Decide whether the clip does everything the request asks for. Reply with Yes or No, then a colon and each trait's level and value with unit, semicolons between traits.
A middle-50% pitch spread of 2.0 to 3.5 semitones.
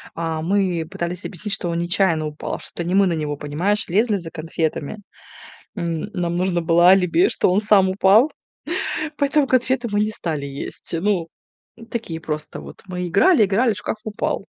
No: average, 3.9 semitones